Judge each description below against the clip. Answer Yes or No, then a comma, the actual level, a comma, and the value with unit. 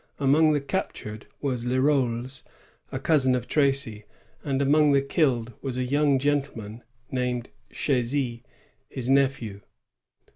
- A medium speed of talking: No, slow, 120 wpm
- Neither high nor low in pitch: No, low, 130 Hz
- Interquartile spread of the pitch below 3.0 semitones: Yes, narrow, 2.6 semitones